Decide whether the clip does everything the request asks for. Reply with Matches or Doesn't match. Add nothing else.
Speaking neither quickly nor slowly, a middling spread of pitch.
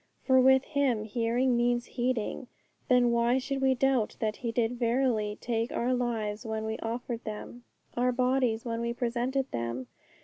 Doesn't match